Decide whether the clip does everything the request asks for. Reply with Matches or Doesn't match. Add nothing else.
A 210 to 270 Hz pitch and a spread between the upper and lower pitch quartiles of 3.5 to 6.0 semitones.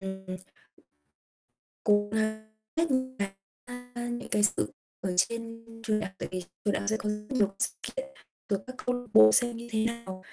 Doesn't match